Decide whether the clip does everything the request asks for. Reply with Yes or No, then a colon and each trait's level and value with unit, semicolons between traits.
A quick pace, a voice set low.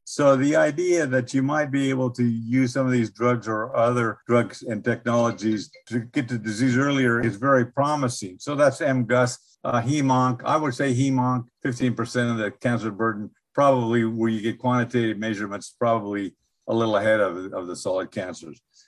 No: average, 180 wpm; low, 125 Hz